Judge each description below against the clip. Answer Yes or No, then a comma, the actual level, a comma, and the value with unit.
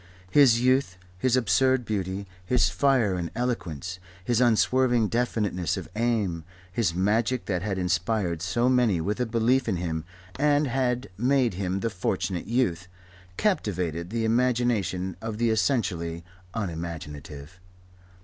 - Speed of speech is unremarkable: No, slow, 130 wpm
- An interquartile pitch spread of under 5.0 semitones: No, wide, 5.4 semitones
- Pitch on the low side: Yes, low, 105 Hz